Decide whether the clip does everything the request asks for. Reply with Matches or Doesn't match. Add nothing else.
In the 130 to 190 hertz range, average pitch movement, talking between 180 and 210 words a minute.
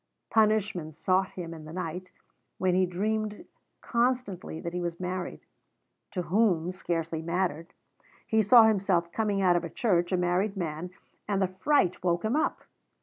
Doesn't match